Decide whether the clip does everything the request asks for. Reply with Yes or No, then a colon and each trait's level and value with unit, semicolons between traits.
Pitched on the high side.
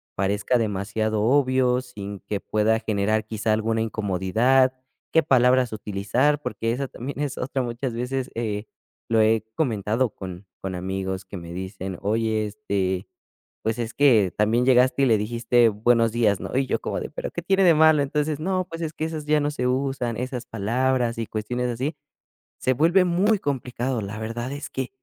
No: low, 120 Hz